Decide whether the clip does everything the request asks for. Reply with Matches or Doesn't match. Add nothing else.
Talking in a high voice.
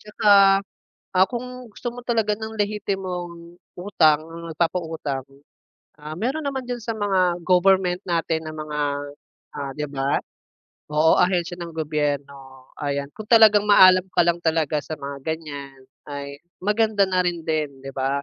Doesn't match